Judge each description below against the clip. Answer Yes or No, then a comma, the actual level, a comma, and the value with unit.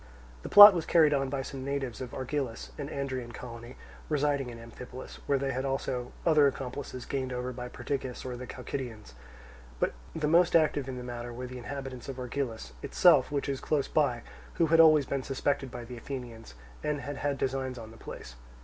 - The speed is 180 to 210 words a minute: Yes, average, 195 wpm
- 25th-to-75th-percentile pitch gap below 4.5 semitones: Yes, narrow, 2.4 semitones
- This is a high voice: No, low, 130 Hz